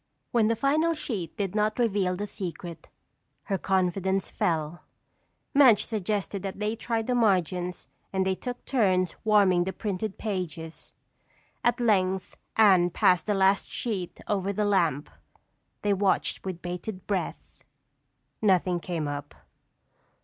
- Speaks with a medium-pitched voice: No, high, 195 Hz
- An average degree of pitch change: Yes, average, 3.0 semitones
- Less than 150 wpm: Yes, slow, 135 wpm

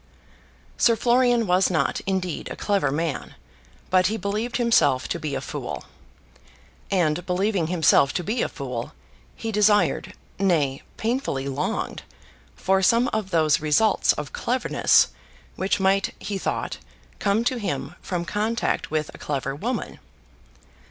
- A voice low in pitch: No, high, 190 Hz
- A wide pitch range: Yes, wide, 6.0 semitones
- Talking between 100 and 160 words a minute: Yes, average, 140 wpm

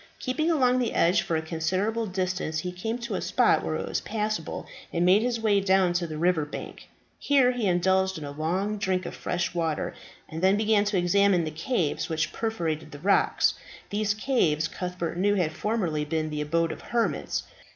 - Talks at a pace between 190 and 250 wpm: Yes, average, 195 wpm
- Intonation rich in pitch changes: No, average, 4.7 semitones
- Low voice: No, medium, 185 Hz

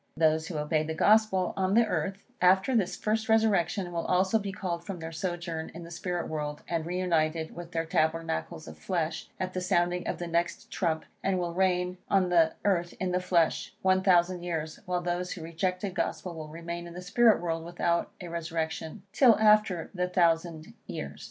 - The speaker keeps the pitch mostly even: Yes, narrow, 2.2 semitones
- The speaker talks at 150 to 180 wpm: No, average, 195 wpm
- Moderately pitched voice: Yes, medium, 175 Hz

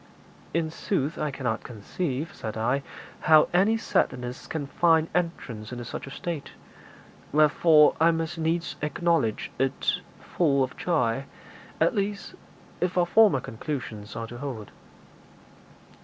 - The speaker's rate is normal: No, slow, 130 wpm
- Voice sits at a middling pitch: Yes, medium, 150 Hz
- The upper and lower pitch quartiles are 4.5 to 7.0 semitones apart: Yes, average, 5.3 semitones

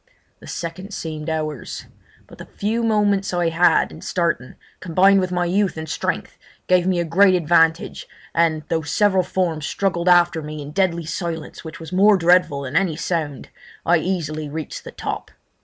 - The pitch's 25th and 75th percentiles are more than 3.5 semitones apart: No, average, 2.7 semitones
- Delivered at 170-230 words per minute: Yes, average, 175 wpm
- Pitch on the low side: No, medium, 170 Hz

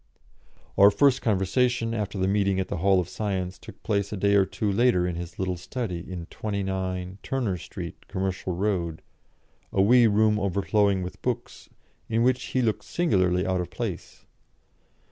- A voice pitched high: No, low, 100 Hz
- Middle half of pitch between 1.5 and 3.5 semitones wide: Yes, average, 2.8 semitones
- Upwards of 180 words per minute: No, average, 165 wpm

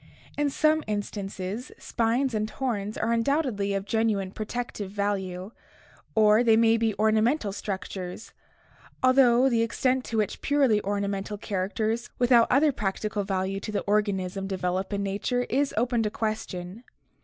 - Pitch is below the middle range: No, high, 215 Hz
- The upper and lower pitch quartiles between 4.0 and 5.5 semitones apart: No, average, 3.2 semitones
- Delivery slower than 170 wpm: Yes, average, 140 wpm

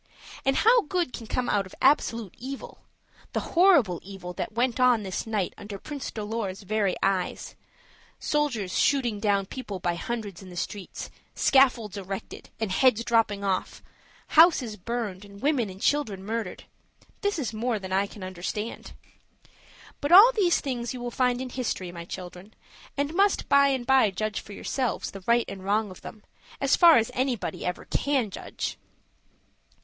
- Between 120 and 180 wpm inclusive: Yes, average, 165 wpm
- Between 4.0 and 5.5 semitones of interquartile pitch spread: Yes, average, 5.1 semitones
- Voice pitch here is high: Yes, high, 225 Hz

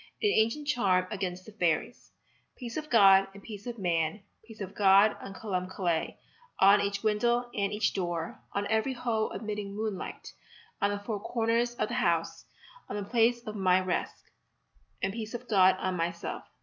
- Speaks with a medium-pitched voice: No, high, 205 Hz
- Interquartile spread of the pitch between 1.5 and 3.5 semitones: Yes, average, 3.2 semitones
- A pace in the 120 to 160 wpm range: No, average, 175 wpm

